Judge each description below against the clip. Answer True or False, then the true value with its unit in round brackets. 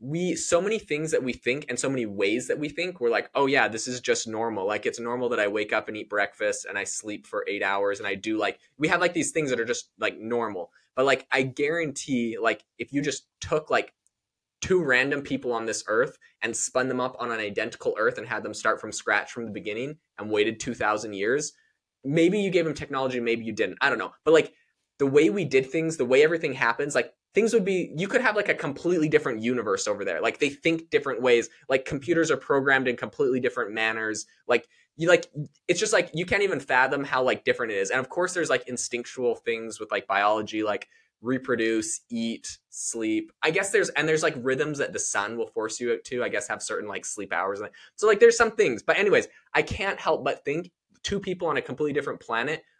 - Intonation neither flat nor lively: False (7.6 semitones)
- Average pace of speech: False (235 wpm)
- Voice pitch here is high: False (145 Hz)